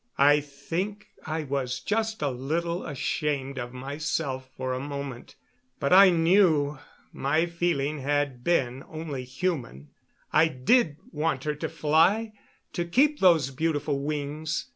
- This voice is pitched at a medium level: Yes, medium, 150 Hz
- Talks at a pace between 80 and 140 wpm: Yes, slow, 135 wpm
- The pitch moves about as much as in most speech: Yes, average, 3.8 semitones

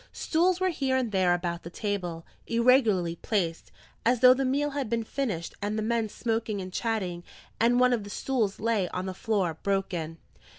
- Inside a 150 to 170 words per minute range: No, average, 185 wpm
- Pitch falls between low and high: No, high, 215 Hz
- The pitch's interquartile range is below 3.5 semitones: No, wide, 5.4 semitones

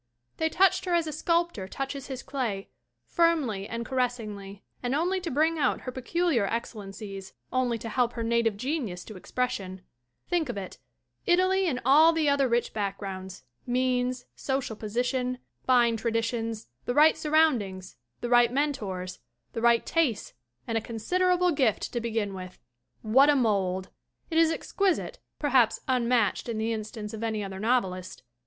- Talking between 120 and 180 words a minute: Yes, average, 160 wpm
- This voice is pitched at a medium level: No, high, 240 Hz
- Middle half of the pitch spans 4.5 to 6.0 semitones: Yes, average, 5.2 semitones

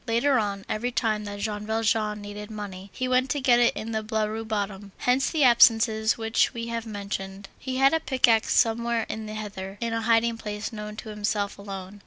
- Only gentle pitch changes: Yes, narrow, 2.1 semitones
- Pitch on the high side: Yes, high, 220 Hz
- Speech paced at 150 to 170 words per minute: No, fast, 205 wpm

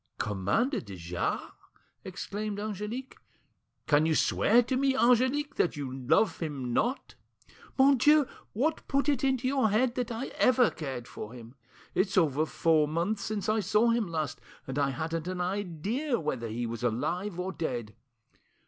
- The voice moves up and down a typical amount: No, wide, 9.0 semitones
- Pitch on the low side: No, high, 190 Hz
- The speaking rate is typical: Yes, average, 160 wpm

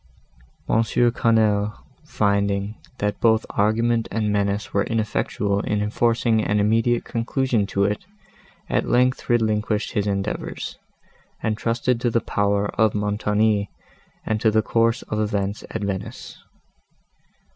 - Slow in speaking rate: Yes, slow, 125 wpm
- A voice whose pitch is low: Yes, low, 105 Hz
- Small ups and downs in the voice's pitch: Yes, narrow, 2.0 semitones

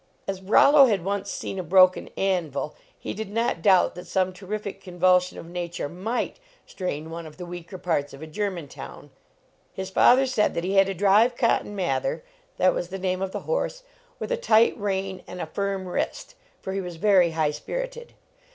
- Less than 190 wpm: No, average, 195 wpm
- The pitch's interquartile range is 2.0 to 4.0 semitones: Yes, average, 2.8 semitones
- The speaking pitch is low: No, high, 190 Hz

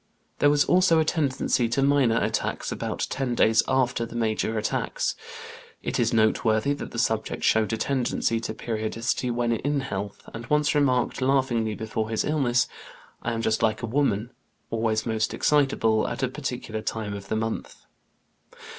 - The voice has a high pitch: No, low, 115 Hz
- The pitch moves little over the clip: No, average, 3.4 semitones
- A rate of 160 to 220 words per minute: Yes, average, 165 wpm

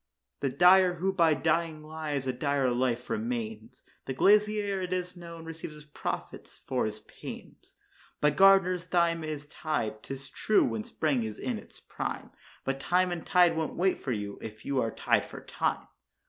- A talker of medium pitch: Yes, medium, 160 Hz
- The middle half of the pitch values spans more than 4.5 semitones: Yes, average, 5.3 semitones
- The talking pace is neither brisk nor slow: Yes, average, 175 wpm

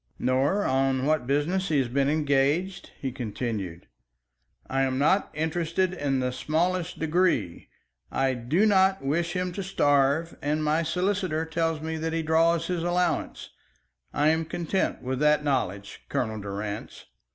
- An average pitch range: Yes, average, 4.3 semitones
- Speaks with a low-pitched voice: No, medium, 155 Hz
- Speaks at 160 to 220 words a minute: No, average, 150 wpm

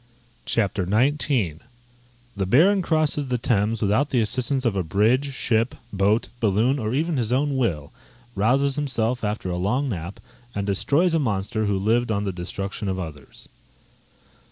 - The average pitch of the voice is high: No, low, 115 Hz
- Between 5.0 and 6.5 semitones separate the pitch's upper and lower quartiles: Yes, average, 5.3 semitones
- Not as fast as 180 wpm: Yes, average, 155 wpm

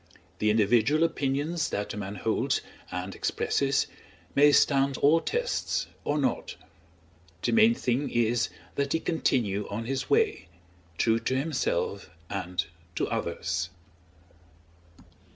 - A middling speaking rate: No, slow, 120 wpm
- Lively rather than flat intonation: Yes, wide, 5.9 semitones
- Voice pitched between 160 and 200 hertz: No, low, 130 Hz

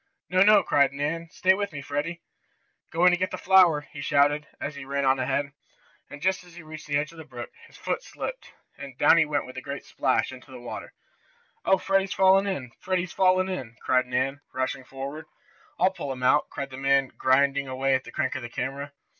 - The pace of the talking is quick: Yes, fast, 220 wpm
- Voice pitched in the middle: Yes, medium, 145 Hz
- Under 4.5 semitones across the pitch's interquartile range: No, average, 5.0 semitones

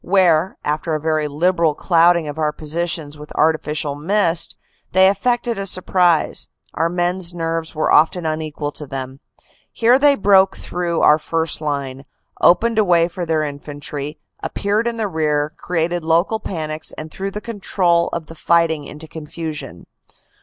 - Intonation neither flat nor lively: Yes, average, 3.1 semitones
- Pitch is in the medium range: Yes, medium, 165 Hz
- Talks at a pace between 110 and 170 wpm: Yes, average, 160 wpm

